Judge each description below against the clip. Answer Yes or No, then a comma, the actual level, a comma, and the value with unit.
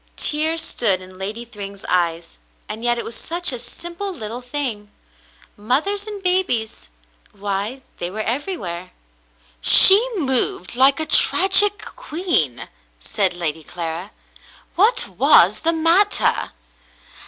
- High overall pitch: Yes, high, 240 Hz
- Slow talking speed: Yes, slow, 125 wpm